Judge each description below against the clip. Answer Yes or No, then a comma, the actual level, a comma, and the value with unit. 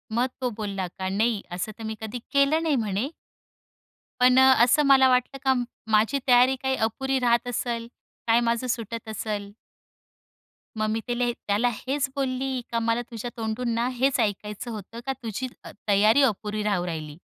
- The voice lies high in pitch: Yes, high, 235 Hz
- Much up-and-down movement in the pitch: No, average, 3.2 semitones